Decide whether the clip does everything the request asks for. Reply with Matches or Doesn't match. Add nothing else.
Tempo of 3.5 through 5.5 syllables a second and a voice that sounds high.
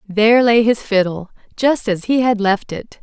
Matches